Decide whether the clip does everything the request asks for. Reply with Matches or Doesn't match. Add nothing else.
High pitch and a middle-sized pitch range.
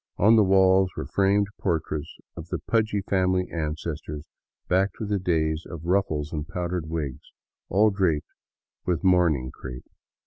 Doesn't match